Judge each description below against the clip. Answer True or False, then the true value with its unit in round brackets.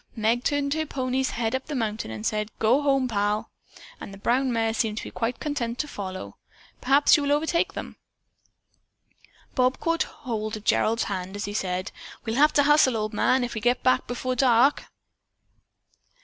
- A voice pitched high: True (240 Hz)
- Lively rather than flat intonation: False (4.1 semitones)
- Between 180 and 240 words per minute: True (190 wpm)